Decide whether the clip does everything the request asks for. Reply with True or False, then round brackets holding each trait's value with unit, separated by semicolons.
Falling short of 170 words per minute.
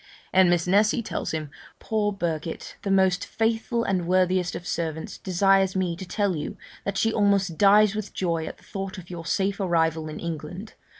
False (185 wpm)